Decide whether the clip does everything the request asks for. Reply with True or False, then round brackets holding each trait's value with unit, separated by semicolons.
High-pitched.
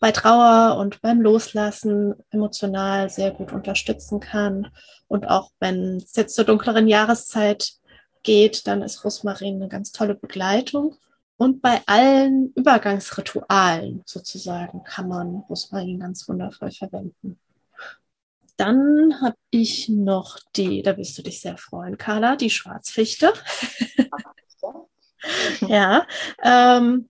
True (215 Hz)